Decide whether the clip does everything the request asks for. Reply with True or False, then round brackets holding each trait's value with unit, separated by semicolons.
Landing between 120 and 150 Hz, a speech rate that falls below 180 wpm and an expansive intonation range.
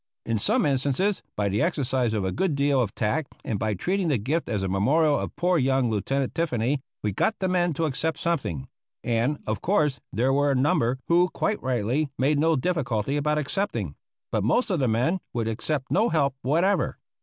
False (140 Hz; 200 wpm; 6.0 semitones)